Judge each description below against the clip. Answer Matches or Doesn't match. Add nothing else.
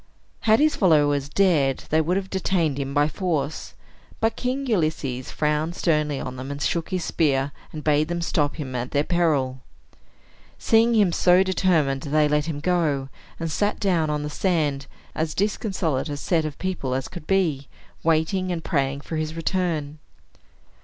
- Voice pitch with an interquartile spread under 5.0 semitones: Matches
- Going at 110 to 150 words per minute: Doesn't match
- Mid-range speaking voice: Matches